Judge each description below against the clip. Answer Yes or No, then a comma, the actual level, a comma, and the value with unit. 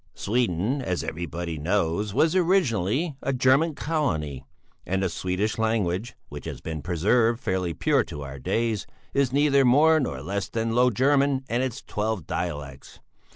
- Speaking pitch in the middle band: No, low, 110 Hz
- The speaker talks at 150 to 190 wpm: Yes, average, 155 wpm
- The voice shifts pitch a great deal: Yes, wide, 7.2 semitones